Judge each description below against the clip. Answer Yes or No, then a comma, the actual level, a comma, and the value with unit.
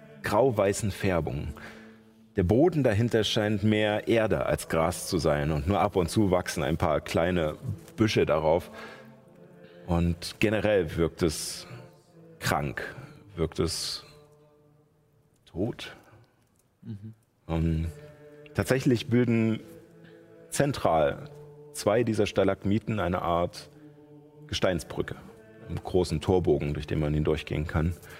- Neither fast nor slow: No, slow, 105 wpm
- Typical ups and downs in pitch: No, wide, 8.7 semitones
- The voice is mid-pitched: No, low, 110 Hz